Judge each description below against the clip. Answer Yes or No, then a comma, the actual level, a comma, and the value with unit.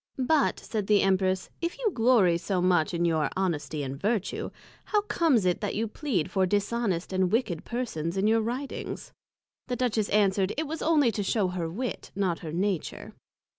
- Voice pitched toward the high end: Yes, high, 200 Hz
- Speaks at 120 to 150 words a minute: No, average, 180 wpm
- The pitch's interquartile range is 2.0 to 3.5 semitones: No, average, 5.0 semitones